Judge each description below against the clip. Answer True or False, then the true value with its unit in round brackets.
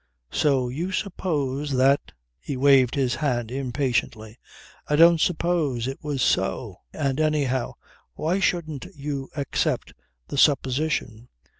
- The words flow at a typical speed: False (125 wpm)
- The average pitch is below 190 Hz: True (140 Hz)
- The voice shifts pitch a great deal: False (3.2 semitones)